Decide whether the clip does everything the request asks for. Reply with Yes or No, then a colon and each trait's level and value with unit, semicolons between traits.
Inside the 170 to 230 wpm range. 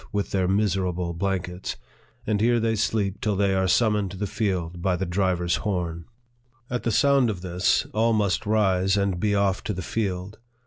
Yes: average, 190 wpm